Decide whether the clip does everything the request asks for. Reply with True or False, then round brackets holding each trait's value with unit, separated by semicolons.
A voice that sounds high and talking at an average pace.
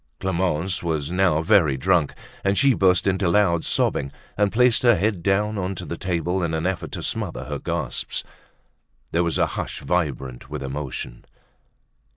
False (90 Hz; 165 wpm)